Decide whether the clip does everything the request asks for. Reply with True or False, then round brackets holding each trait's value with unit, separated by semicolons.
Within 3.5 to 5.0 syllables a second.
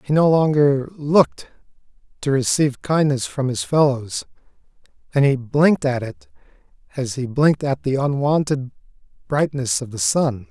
True (4.8 syllables/s)